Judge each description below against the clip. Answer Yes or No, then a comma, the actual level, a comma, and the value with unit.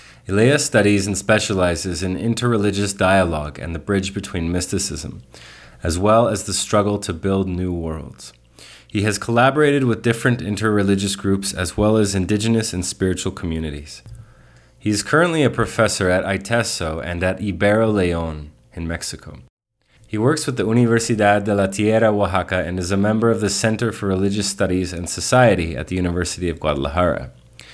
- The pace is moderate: Yes, average, 160 wpm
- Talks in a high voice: No, low, 100 Hz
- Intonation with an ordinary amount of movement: Yes, average, 3.4 semitones